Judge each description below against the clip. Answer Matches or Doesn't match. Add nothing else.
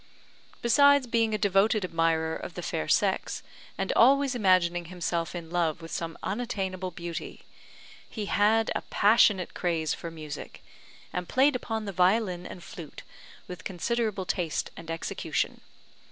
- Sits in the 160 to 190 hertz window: Matches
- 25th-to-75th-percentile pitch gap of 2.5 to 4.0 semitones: Doesn't match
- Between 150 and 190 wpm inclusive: Doesn't match